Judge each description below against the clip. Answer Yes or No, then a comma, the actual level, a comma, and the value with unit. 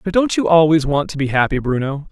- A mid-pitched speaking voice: Yes, medium, 160 Hz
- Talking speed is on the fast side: Yes, fast, 255 wpm